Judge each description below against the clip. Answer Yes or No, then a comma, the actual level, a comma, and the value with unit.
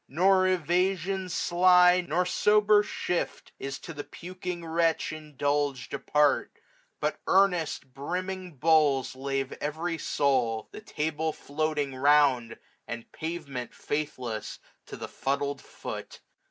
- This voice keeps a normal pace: No, slow, 120 wpm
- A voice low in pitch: No, medium, 155 Hz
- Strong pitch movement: No, average, 4.3 semitones